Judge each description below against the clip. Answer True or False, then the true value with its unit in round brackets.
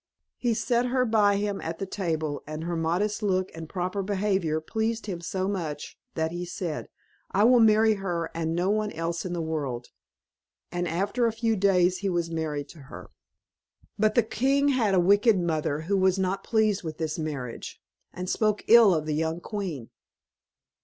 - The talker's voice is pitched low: False (185 Hz)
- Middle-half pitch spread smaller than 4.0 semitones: False (4.5 semitones)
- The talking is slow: False (185 wpm)